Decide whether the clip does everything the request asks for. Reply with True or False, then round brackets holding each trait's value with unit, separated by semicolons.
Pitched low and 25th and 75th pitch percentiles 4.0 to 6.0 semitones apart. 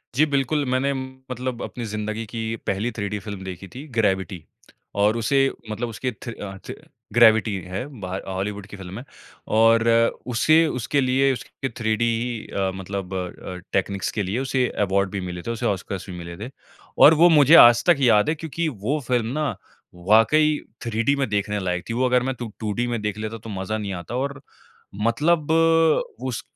True (115 Hz; 4.5 semitones)